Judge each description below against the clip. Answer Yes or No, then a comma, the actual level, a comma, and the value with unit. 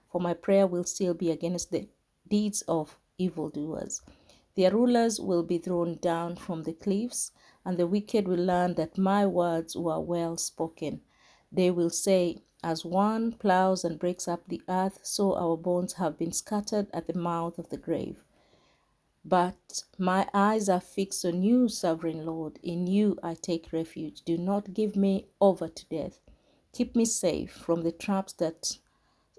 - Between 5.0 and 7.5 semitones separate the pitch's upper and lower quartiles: No, average, 2.7 semitones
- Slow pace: No, average, 165 wpm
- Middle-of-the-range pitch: Yes, medium, 180 Hz